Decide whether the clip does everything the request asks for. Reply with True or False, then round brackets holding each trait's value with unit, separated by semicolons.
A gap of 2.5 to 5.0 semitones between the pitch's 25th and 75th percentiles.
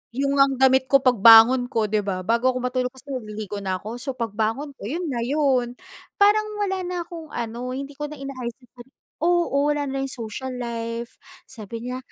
True (3.3 semitones)